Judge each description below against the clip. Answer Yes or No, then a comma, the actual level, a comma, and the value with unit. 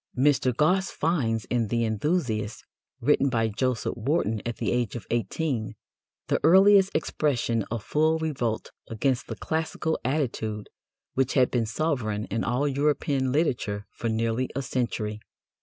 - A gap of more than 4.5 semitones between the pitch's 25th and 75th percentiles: Yes, average, 4.9 semitones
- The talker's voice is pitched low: Yes, low, 125 Hz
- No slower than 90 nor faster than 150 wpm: Yes, average, 140 wpm